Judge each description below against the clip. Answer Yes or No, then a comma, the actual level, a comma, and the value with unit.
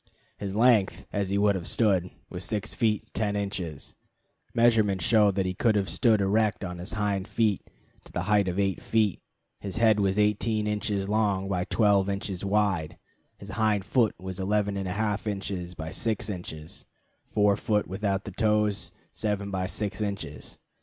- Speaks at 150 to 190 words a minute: Yes, average, 165 wpm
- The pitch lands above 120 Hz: No, low, 100 Hz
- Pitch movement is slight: Yes, narrow, 1.9 semitones